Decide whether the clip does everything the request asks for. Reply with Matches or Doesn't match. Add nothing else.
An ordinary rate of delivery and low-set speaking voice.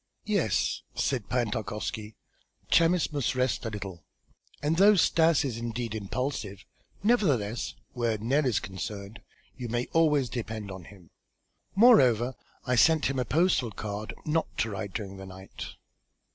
Matches